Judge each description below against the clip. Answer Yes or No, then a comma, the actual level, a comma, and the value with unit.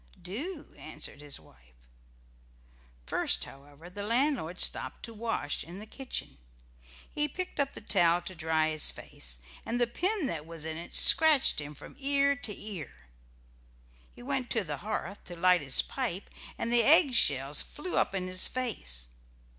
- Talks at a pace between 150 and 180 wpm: Yes, average, 165 wpm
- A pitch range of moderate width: No, wide, 8.3 semitones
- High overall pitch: Yes, high, 195 Hz